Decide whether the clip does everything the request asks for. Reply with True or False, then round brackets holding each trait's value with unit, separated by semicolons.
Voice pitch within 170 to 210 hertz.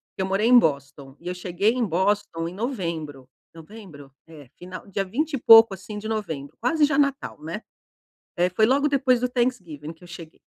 True (190 Hz)